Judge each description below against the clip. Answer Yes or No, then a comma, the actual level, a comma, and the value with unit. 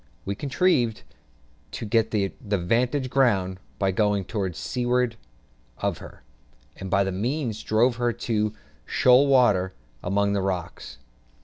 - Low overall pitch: Yes, low, 110 Hz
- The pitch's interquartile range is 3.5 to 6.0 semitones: Yes, average, 4.2 semitones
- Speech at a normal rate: No, slow, 130 wpm